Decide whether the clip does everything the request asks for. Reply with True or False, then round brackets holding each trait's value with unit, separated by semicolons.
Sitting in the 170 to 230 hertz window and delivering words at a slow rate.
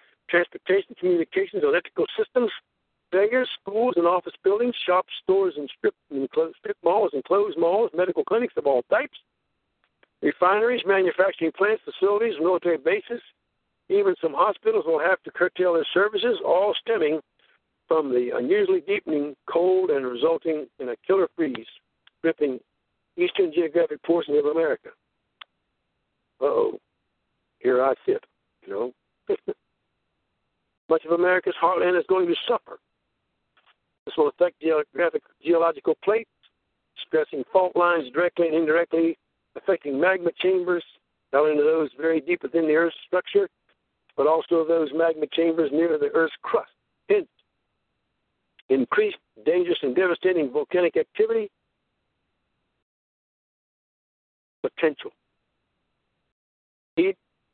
True (190 Hz; 115 wpm)